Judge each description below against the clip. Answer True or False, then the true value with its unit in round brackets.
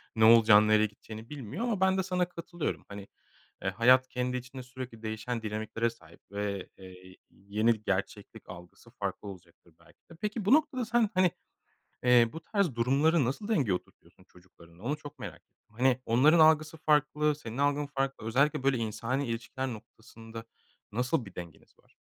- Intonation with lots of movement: True (5.7 semitones)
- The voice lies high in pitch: False (120 Hz)